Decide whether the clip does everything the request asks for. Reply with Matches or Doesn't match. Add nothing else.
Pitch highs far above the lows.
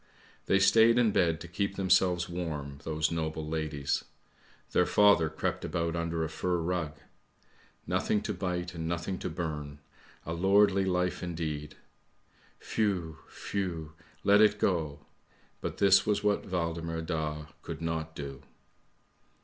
Doesn't match